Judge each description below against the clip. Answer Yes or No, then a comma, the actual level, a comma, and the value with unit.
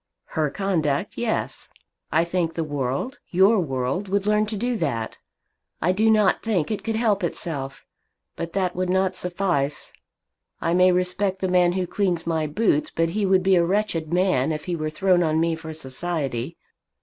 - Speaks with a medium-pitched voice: Yes, medium, 180 Hz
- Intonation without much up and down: No, average, 3.5 semitones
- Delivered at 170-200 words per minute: Yes, average, 180 wpm